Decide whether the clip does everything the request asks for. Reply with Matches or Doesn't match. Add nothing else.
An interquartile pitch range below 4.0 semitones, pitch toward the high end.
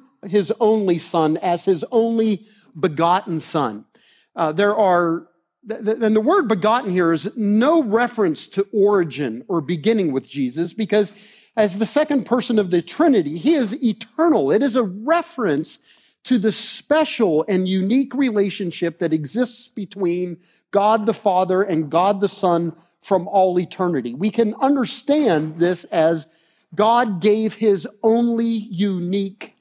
Doesn't match